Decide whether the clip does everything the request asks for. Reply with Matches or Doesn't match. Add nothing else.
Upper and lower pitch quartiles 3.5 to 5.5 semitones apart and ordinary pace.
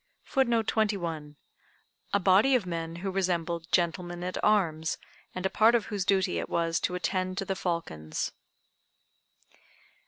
Doesn't match